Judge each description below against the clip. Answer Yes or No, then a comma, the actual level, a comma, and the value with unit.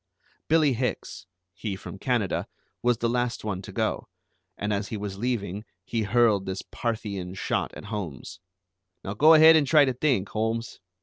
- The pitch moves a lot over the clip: No, average, 3.7 semitones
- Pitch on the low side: Yes, low, 110 Hz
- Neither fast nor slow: Yes, average, 170 wpm